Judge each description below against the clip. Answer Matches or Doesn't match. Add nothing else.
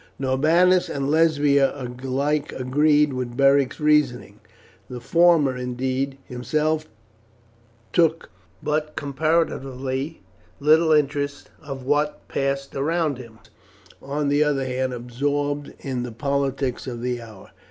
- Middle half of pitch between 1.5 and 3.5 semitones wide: Matches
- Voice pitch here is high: Doesn't match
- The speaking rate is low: Matches